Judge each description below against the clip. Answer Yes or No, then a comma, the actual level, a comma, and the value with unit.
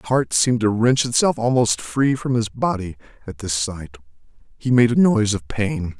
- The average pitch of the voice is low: Yes, low, 115 Hz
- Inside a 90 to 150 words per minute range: No, average, 200 wpm